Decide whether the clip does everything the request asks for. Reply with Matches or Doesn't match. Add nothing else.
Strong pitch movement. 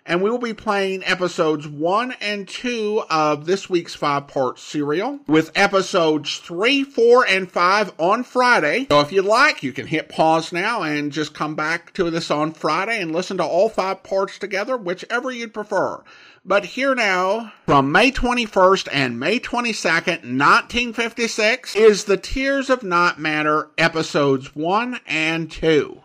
Matches